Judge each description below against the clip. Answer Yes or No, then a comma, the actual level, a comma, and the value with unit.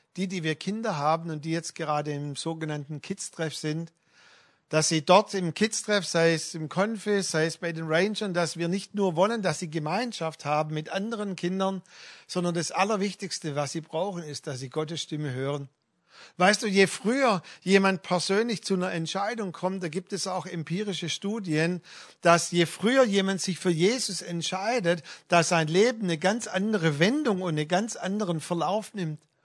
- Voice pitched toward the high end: No, medium, 175 Hz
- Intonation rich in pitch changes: No, average, 3.4 semitones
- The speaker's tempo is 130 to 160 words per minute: No, average, 180 wpm